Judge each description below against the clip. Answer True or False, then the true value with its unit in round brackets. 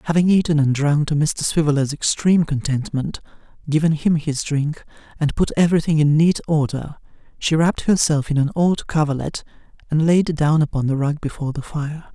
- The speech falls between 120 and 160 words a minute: False (175 wpm)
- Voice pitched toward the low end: False (155 Hz)